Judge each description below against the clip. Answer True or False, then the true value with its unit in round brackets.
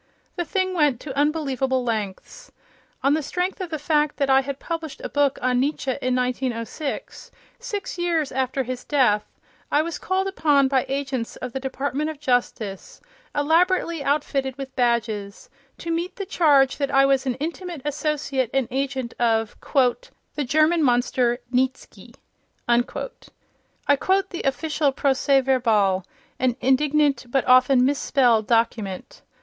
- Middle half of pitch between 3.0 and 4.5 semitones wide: True (3.3 semitones)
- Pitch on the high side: True (270 Hz)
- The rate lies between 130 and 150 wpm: True (145 wpm)